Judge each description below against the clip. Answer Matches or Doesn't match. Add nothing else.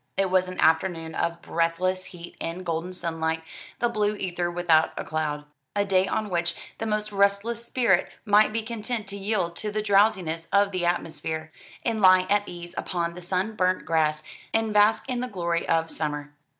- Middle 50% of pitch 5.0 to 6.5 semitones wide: Doesn't match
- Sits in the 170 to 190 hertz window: Matches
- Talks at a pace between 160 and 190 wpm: Matches